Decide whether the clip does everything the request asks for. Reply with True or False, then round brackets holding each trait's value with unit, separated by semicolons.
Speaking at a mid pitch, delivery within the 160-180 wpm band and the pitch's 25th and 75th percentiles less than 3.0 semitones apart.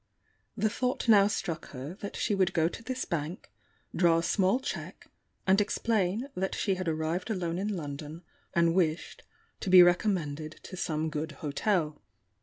False (180 Hz; 165 wpm; 4.1 semitones)